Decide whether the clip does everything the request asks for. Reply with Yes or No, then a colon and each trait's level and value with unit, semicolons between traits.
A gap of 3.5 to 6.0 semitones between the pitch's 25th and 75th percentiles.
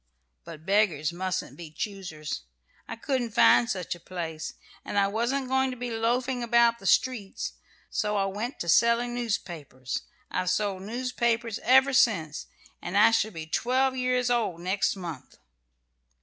Yes: average, 5.1 semitones